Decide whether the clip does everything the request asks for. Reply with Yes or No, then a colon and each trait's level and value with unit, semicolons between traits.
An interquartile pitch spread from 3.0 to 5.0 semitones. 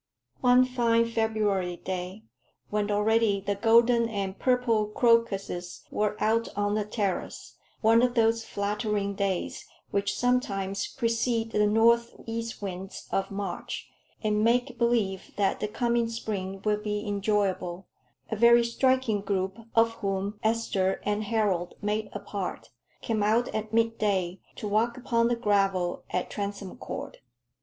No: narrow, 2.6 semitones